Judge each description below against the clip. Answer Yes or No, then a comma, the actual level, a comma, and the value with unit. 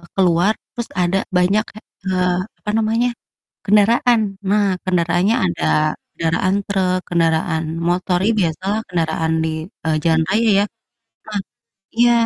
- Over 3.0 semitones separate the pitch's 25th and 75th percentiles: Yes, average, 3.9 semitones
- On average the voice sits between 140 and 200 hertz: Yes, medium, 185 Hz